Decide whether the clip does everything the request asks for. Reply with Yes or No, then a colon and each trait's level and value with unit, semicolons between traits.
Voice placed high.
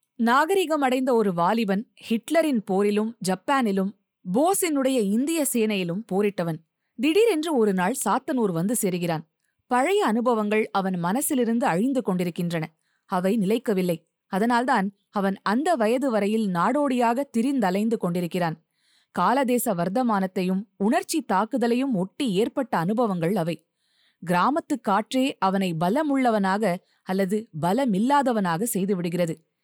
Yes: high, 215 Hz